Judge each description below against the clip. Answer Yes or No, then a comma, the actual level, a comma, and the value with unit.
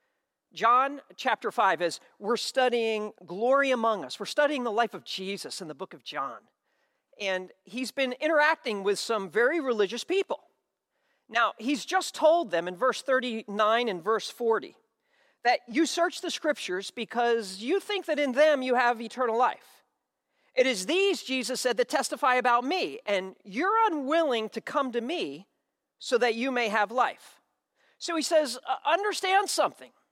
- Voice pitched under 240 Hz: No, very high, 250 Hz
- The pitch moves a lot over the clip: Yes, wide, 5.7 semitones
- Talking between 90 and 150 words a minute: No, average, 165 wpm